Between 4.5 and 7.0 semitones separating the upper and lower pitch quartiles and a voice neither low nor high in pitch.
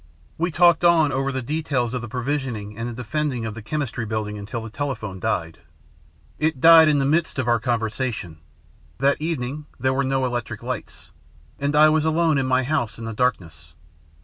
No: average, 4.8 semitones; low, 130 Hz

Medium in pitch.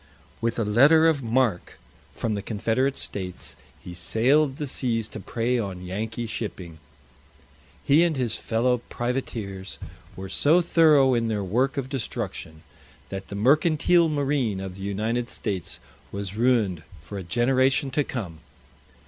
No: low, 115 Hz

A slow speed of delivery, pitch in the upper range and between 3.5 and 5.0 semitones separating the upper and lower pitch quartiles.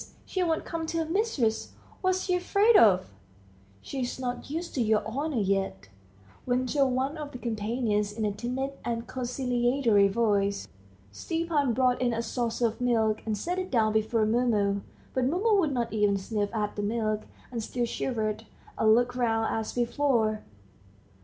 No: average, 165 wpm; high, 240 Hz; average, 4.0 semitones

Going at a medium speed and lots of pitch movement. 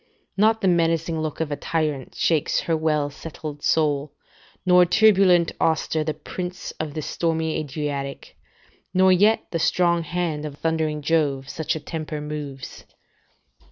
No: average, 145 wpm; narrow, 2.5 semitones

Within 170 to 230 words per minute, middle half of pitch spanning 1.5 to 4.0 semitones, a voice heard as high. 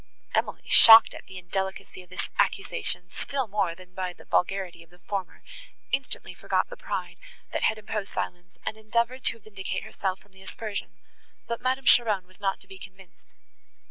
Yes: average, 175 wpm; average, 3.2 semitones; high, 195 Hz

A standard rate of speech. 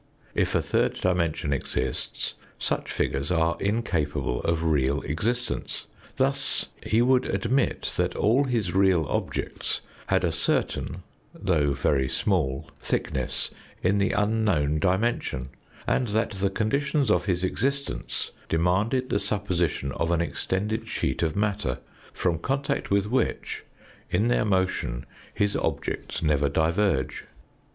No: slow, 130 wpm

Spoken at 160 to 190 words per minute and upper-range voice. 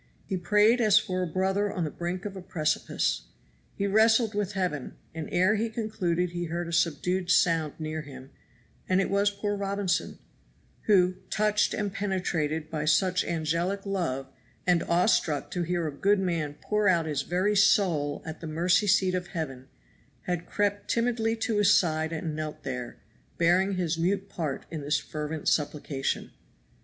No: average, 170 wpm; medium, 180 Hz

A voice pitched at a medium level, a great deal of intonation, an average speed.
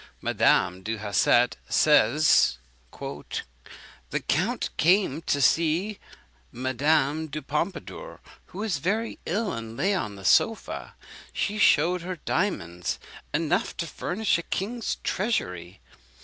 No: medium, 155 Hz; wide, 8.4 semitones; slow, 115 wpm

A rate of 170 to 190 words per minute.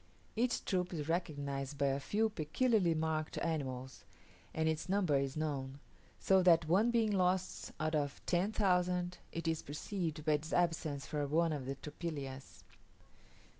No: average, 155 wpm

